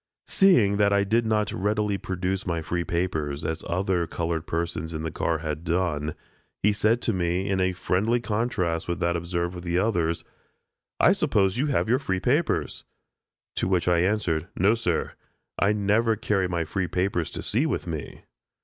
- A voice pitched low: Yes, very low, 90 Hz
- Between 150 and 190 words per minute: Yes, average, 185 wpm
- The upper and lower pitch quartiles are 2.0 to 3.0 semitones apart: No, average, 3.7 semitones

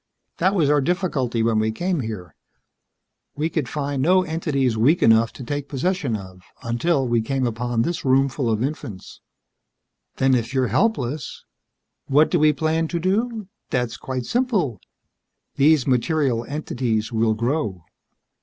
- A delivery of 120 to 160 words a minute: Yes, average, 150 wpm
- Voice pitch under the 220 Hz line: Yes, low, 135 Hz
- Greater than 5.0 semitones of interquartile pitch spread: Yes, wide, 5.4 semitones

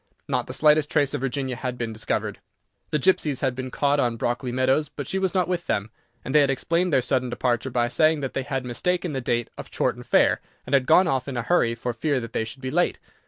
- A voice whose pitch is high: No, low, 130 Hz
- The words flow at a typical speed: No, fast, 245 wpm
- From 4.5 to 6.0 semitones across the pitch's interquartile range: No, average, 3.6 semitones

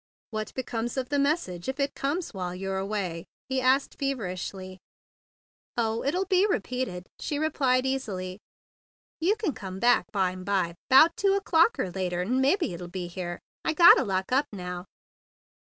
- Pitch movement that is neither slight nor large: No, wide, 7.2 semitones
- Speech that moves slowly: No, average, 155 wpm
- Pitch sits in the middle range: No, high, 230 Hz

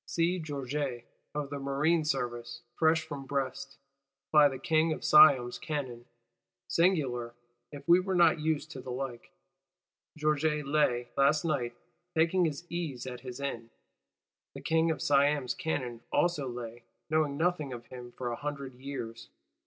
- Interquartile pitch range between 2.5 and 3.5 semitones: No, average, 4.0 semitones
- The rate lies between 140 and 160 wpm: Yes, average, 150 wpm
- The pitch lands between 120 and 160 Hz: Yes, medium, 140 Hz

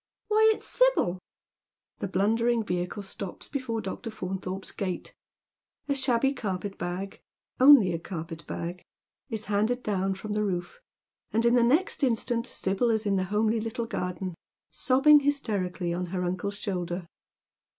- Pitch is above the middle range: Yes, high, 205 Hz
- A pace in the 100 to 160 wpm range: Yes, average, 155 wpm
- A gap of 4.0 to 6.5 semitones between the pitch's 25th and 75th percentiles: Yes, average, 4.5 semitones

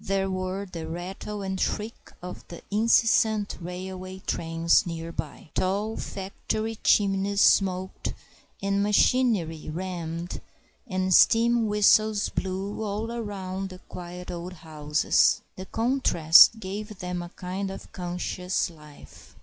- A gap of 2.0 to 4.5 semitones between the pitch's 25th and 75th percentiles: Yes, average, 2.7 semitones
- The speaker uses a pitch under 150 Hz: No, high, 190 Hz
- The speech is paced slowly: Yes, slow, 120 wpm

